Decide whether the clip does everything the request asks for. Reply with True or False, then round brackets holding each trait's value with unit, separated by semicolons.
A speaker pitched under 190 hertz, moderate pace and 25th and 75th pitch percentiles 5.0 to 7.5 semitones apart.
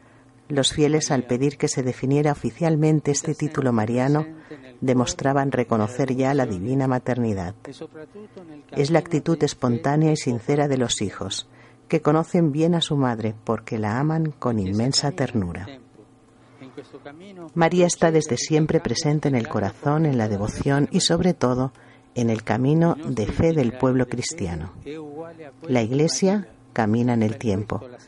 False (135 Hz; 140 wpm; 4.3 semitones)